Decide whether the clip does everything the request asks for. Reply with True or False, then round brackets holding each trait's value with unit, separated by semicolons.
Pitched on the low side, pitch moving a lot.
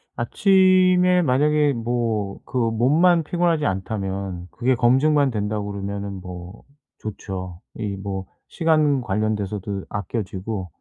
True (115 Hz; 7.2 semitones)